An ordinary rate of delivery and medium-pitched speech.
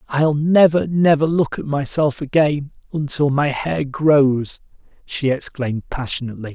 No: slow, 130 wpm; medium, 145 Hz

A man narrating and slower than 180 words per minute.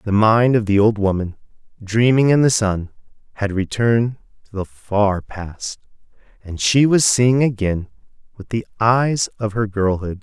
Yes: male; average, 160 wpm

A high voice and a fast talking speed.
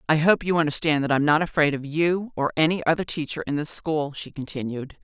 No: medium, 155 Hz; fast, 240 wpm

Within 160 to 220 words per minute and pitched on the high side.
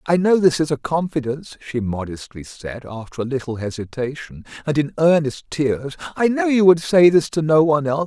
No: average, 200 wpm; medium, 145 Hz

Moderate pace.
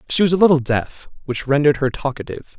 No: fast, 210 wpm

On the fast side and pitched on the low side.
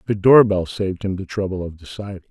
Yes: fast, 235 wpm; very low, 95 Hz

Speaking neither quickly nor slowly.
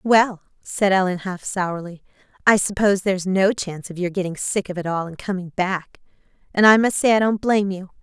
No: fast, 210 wpm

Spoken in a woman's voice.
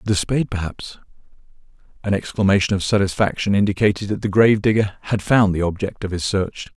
No: male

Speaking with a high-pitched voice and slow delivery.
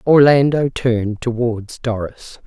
No: low, 120 Hz; slow, 95 wpm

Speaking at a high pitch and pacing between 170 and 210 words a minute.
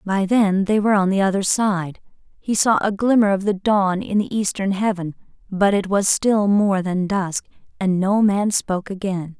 Yes: high, 195 Hz; average, 200 wpm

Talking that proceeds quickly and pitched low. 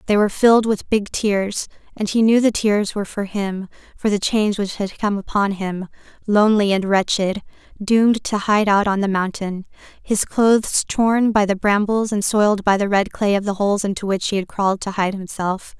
No: fast, 210 wpm; high, 205 Hz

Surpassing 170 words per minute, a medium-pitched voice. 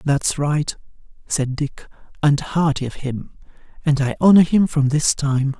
No: average, 160 wpm; medium, 145 Hz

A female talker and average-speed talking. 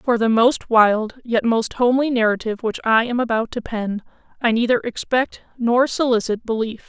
Yes: female; average, 175 wpm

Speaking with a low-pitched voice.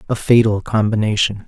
Yes: low, 105 Hz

